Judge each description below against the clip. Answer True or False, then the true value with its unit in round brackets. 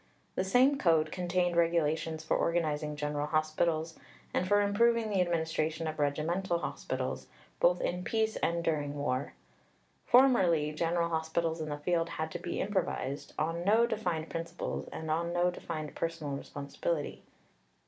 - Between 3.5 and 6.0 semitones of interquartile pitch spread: False (2.5 semitones)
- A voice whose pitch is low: False (165 Hz)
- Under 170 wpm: True (145 wpm)